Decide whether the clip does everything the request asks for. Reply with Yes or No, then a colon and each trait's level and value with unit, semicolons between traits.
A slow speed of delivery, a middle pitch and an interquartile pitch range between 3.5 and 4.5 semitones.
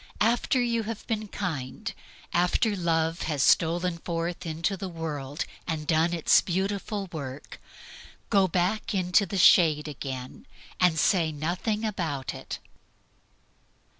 Yes: slow, 125 wpm; medium, 175 Hz; average, 3.8 semitones